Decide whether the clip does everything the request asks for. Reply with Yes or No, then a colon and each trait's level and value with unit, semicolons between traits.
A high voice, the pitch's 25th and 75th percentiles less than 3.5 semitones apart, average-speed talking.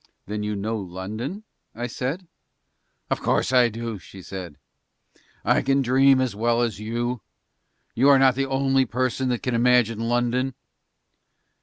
No: low, 120 Hz; average, 3.1 semitones; average, 150 wpm